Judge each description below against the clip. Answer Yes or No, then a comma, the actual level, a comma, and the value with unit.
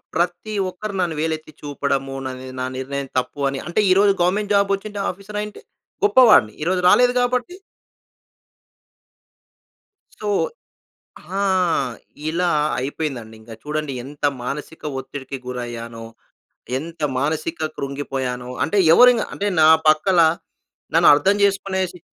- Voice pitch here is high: No, medium, 160 Hz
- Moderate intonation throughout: No, wide, 6.6 semitones